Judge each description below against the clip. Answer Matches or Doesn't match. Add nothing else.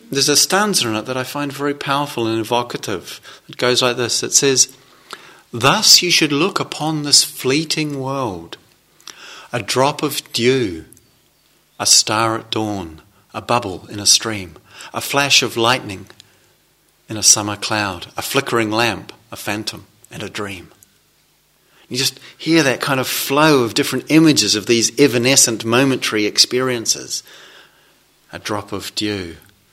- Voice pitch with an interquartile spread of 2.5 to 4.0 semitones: Doesn't match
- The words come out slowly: Doesn't match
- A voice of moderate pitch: Doesn't match